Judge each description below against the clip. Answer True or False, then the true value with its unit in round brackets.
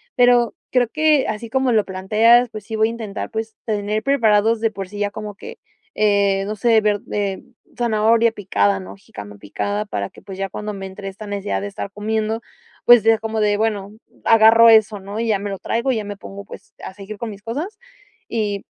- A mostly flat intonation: True (2.1 semitones)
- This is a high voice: True (215 Hz)